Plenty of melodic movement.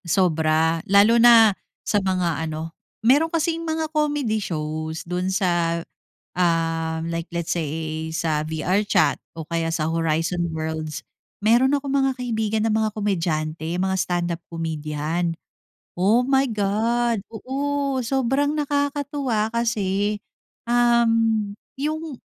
Yes: wide, 6.6 semitones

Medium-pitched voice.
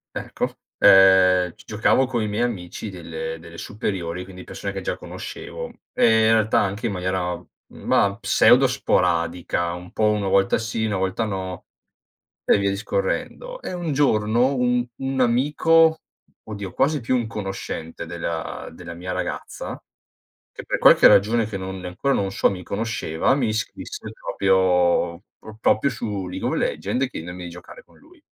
No: low, 100 Hz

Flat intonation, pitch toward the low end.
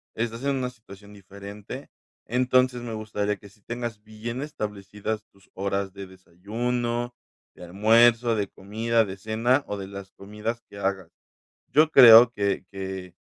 No: average, 3.3 semitones; low, 110 Hz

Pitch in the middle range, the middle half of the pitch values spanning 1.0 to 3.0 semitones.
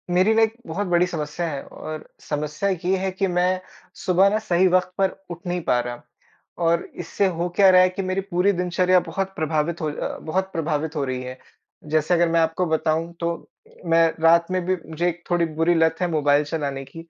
Yes: medium, 170 Hz; narrow, 2.6 semitones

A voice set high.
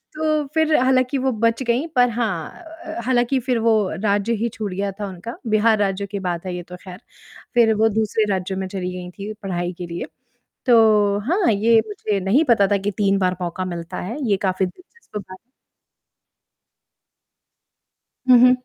Yes: high, 210 Hz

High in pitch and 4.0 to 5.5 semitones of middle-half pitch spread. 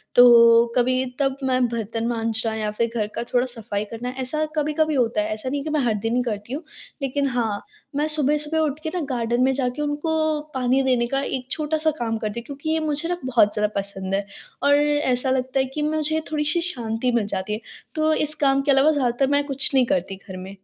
Yes: very high, 260 Hz; average, 4.4 semitones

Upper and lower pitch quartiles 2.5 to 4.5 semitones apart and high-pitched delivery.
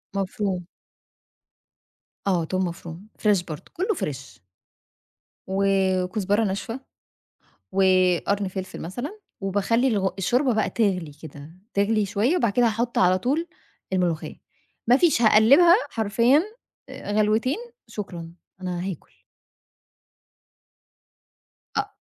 Yes: average, 4.1 semitones; high, 200 Hz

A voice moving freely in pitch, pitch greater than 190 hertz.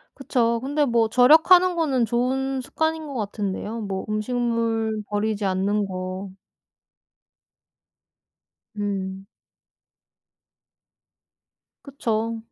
No: average, 4.4 semitones; high, 230 Hz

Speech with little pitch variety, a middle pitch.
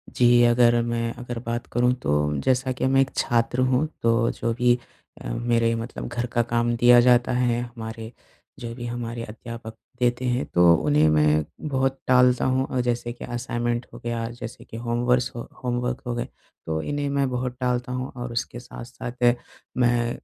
No: narrow, 1.2 semitones; low, 120 Hz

